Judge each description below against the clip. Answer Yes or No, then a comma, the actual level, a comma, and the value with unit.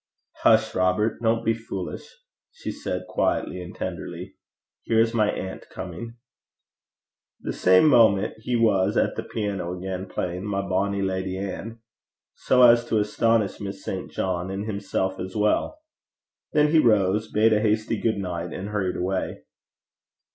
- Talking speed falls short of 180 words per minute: Yes, average, 155 wpm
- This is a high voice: No, low, 100 Hz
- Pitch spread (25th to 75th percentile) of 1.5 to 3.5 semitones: Yes, average, 3.1 semitones